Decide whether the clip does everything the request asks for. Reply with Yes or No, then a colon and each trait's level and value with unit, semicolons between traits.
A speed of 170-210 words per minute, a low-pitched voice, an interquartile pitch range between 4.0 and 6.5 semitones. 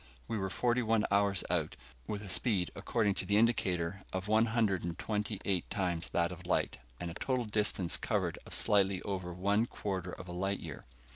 No: average, 200 wpm; low, 100 Hz; average, 2.9 semitones